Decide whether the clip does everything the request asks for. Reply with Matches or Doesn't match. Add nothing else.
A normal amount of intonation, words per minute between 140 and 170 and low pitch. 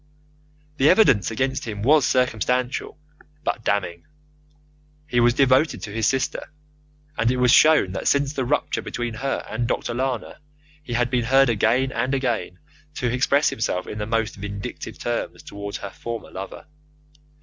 Matches